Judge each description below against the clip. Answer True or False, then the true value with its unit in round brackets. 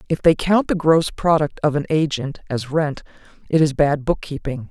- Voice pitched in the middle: True (150 Hz)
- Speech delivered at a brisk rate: False (190 wpm)